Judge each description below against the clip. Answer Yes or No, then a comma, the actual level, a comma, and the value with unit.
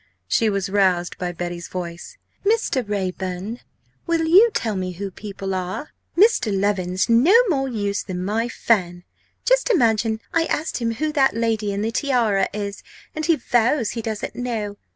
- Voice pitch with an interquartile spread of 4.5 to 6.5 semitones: Yes, average, 5.1 semitones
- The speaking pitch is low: No, high, 215 Hz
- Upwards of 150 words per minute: Yes, average, 165 wpm